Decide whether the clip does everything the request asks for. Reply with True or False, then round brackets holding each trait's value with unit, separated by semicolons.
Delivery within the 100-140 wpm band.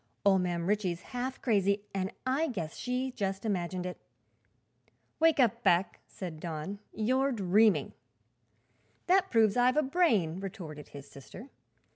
True (135 wpm)